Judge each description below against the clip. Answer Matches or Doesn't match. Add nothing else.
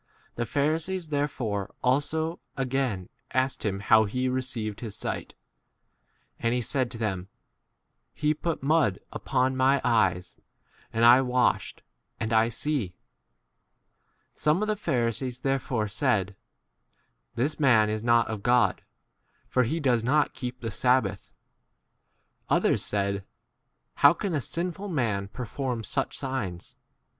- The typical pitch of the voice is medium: Doesn't match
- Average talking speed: Doesn't match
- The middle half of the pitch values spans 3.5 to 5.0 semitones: Matches